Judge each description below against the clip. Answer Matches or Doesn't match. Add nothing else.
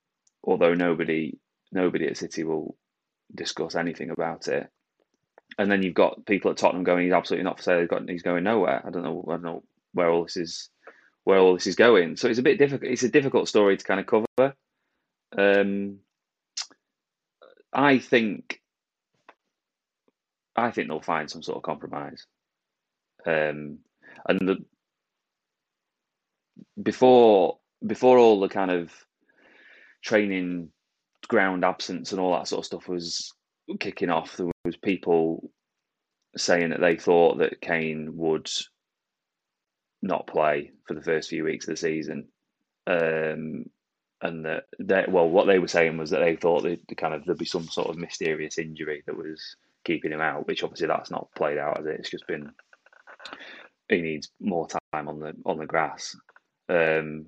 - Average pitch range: Matches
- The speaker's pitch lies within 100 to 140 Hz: Doesn't match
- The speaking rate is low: Doesn't match